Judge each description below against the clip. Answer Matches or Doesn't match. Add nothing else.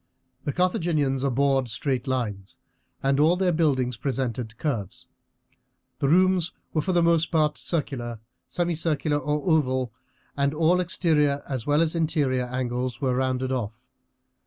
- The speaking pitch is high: Doesn't match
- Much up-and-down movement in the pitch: Doesn't match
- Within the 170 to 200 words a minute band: Doesn't match